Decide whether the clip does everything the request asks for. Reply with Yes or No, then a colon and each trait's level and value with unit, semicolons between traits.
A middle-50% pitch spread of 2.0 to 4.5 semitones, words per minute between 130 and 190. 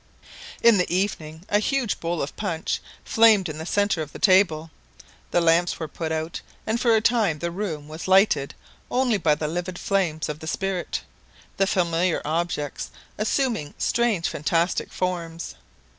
Yes: average, 4.2 semitones; average, 160 wpm